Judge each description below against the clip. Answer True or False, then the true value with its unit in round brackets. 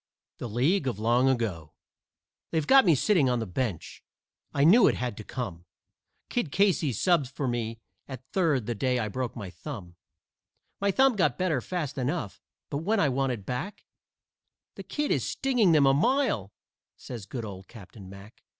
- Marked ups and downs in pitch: True (7.3 semitones)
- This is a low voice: True (130 Hz)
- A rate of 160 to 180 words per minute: True (175 wpm)